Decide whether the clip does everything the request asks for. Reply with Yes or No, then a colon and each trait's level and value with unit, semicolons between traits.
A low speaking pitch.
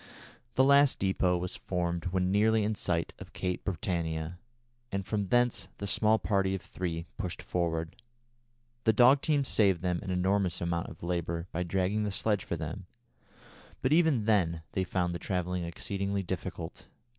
Yes: very low, 95 Hz